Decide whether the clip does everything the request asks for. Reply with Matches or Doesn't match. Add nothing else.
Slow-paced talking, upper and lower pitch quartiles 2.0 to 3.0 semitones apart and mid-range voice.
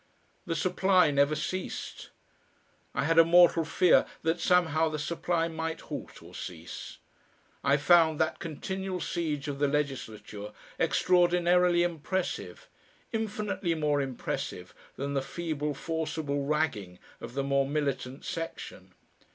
Doesn't match